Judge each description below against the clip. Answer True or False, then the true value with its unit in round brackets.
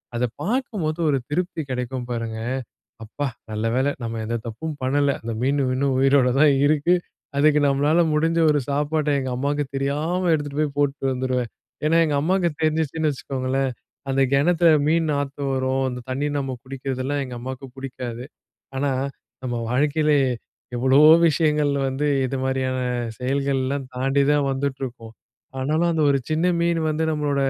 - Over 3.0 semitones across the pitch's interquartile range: False (2.7 semitones)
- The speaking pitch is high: False (140 Hz)